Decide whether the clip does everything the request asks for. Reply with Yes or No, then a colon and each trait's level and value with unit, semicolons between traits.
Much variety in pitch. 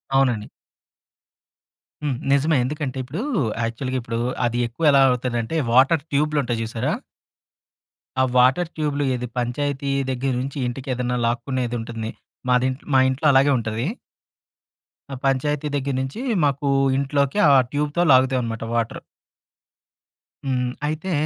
No: average, 2.8 semitones